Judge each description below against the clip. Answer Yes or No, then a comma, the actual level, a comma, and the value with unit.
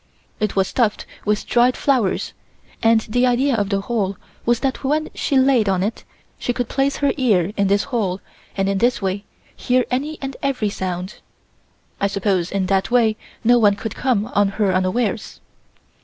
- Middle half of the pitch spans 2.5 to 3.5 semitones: No, average, 4.2 semitones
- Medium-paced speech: Yes, average, 180 wpm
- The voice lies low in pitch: No, high, 215 Hz